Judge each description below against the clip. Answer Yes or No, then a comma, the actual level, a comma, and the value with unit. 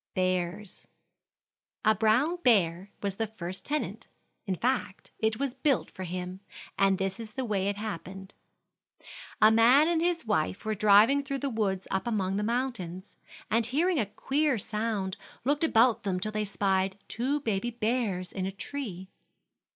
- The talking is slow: No, average, 160 wpm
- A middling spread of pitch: Yes, average, 4.6 semitones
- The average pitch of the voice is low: No, high, 215 Hz